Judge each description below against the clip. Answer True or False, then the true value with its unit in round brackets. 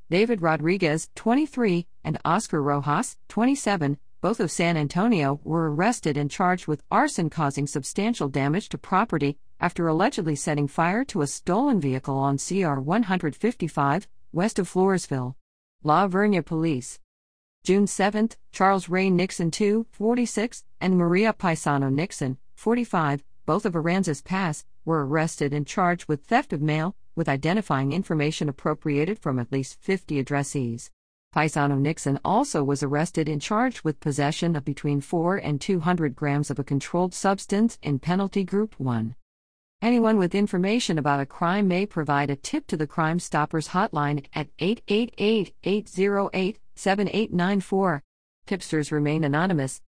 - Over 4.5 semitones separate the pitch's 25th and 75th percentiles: True (5.2 semitones)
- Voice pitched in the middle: True (165 Hz)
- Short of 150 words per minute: True (140 wpm)